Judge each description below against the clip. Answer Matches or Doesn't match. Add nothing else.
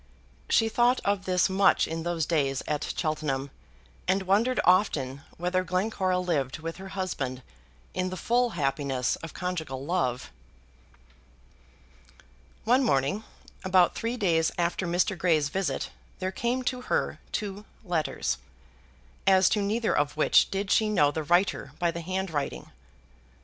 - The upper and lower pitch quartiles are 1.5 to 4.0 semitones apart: Doesn't match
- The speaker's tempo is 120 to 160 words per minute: Matches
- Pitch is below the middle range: Doesn't match